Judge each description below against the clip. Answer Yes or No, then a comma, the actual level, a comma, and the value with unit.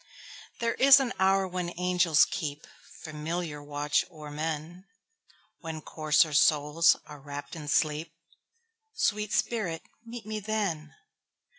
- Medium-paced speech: No, slow, 105 wpm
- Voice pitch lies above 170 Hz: No, medium, 165 Hz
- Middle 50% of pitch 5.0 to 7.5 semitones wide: Yes, average, 5.3 semitones